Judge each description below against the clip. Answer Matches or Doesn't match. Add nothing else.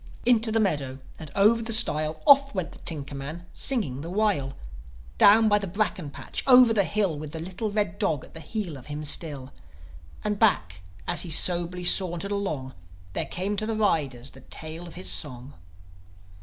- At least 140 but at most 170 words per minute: Doesn't match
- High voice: Doesn't match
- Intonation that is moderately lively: Doesn't match